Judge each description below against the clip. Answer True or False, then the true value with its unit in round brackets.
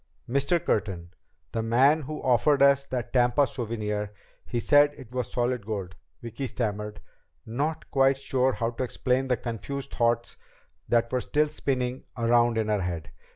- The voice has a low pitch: True (120 Hz)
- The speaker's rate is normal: True (160 wpm)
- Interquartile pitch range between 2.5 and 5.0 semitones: True (3.2 semitones)